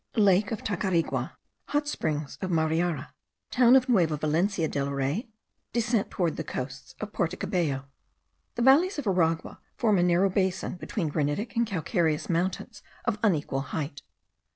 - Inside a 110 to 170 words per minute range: Yes, average, 150 wpm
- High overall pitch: No, medium, 175 Hz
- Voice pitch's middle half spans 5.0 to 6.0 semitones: Yes, wide, 5.4 semitones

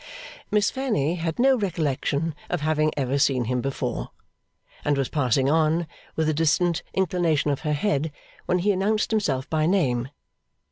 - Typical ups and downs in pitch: Yes, average, 4.3 semitones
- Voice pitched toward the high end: No, medium, 155 Hz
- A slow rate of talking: No, average, 155 wpm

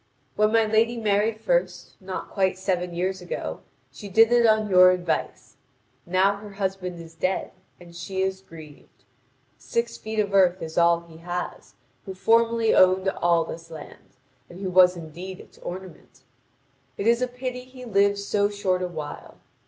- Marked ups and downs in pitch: No, average, 3.4 semitones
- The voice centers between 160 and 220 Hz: Yes, high, 190 Hz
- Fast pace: No, average, 170 wpm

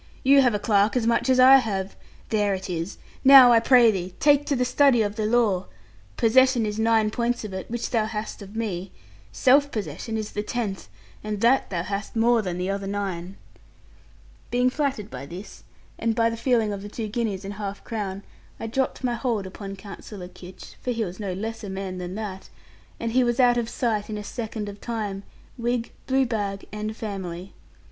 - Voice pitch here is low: No, high, 215 Hz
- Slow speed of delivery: No, fast, 205 wpm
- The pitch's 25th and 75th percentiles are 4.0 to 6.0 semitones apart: No, average, 3.3 semitones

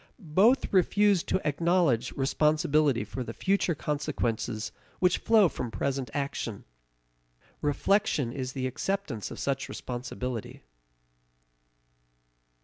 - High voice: No, medium, 145 Hz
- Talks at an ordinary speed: No, slow, 100 wpm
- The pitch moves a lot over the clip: Yes, wide, 6.2 semitones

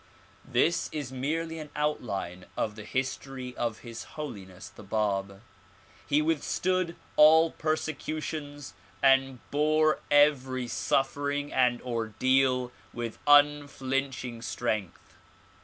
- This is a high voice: No, low, 135 Hz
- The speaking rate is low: Yes, slow, 100 wpm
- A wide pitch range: No, average, 4.1 semitones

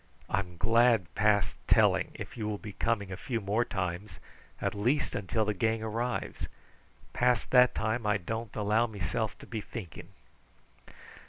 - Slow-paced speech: No, average, 155 wpm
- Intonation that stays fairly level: Yes, narrow, 2.3 semitones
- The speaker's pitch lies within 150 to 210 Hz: No, low, 110 Hz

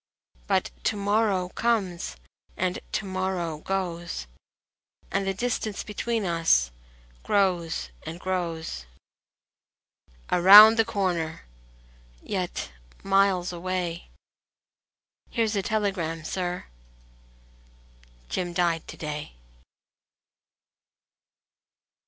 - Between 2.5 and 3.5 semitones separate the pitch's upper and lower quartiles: Yes, average, 3.2 semitones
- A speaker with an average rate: No, slow, 85 wpm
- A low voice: No, medium, 180 Hz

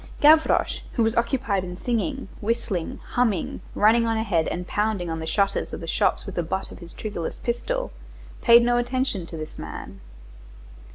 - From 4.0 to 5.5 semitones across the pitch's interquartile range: Yes, average, 5.2 semitones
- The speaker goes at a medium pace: Yes, average, 175 wpm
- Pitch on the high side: Yes, high, 220 Hz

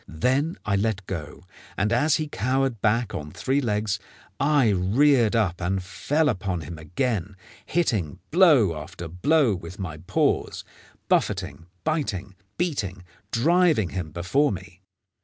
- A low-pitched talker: Yes, low, 105 Hz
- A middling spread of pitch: No, wide, 7.1 semitones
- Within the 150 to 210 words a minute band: No, slow, 135 wpm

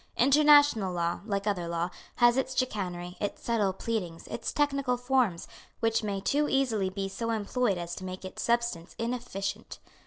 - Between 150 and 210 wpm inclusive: Yes, average, 160 wpm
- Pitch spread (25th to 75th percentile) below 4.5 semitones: No, average, 4.9 semitones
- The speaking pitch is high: Yes, high, 215 Hz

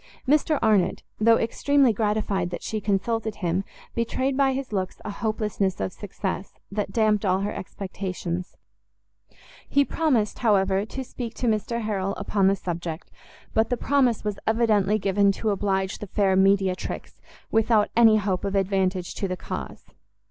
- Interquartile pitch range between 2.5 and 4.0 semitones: Yes, average, 2.8 semitones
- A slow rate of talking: No, average, 155 wpm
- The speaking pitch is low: No, high, 205 Hz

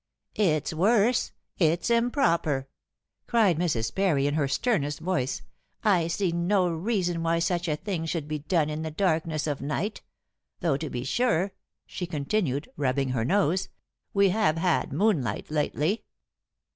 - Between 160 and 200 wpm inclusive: No, average, 145 wpm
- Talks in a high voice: No, medium, 165 Hz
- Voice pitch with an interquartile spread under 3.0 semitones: No, average, 4.7 semitones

